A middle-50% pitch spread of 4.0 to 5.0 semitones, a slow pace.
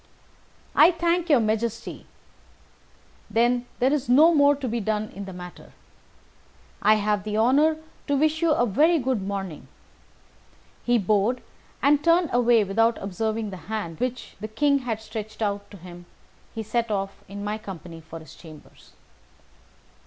No: average, 4.5 semitones; average, 155 wpm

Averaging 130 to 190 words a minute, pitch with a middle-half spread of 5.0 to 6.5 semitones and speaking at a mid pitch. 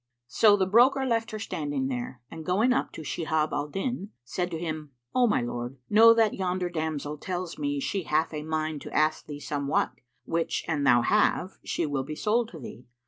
No: average, 200 wpm; average, 5.3 semitones; medium, 160 Hz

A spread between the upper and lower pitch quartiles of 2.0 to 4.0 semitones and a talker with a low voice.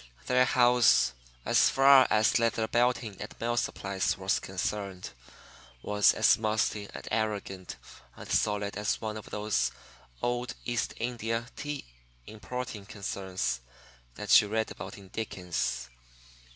Yes: average, 3.2 semitones; low, 110 Hz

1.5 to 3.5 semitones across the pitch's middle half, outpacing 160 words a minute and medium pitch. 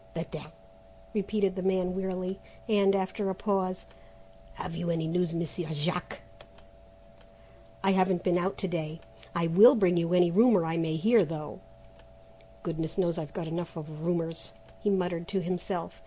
No: narrow, 2.5 semitones; average, 155 wpm; medium, 180 Hz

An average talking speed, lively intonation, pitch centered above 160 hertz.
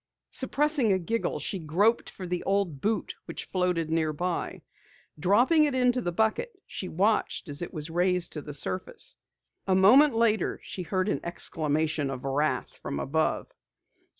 Yes: average, 155 wpm; wide, 5.7 semitones; medium, 185 Hz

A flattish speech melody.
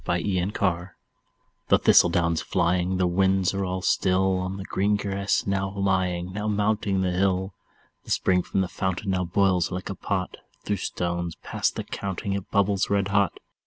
Yes: narrow, 1.4 semitones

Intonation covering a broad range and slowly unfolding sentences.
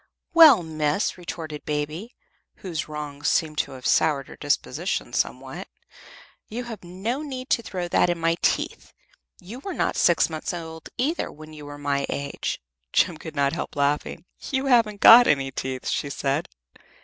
No: wide, 6.4 semitones; average, 165 wpm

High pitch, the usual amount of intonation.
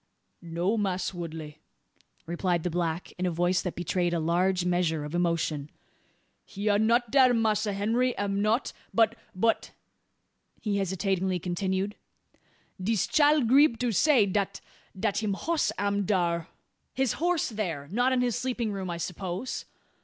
Yes: high, 195 Hz; average, 4.4 semitones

